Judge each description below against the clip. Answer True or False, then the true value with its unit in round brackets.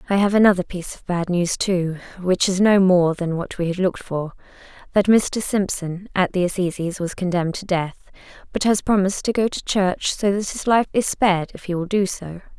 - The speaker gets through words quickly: True (215 wpm)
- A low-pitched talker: False (185 Hz)